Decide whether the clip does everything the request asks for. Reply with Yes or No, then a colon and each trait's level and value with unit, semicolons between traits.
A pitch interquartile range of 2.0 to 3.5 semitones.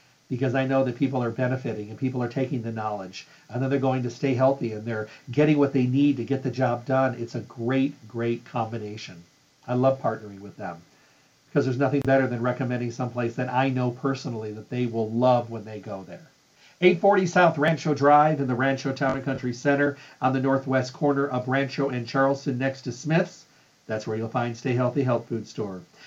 Yes: narrow, 2.6 semitones